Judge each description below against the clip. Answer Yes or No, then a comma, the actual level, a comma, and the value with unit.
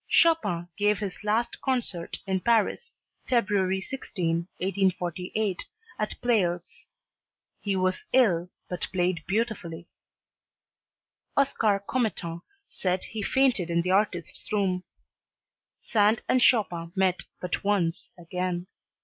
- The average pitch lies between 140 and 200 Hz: Yes, high, 190 Hz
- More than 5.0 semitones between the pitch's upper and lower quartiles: No, average, 3.6 semitones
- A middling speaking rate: No, slow, 105 wpm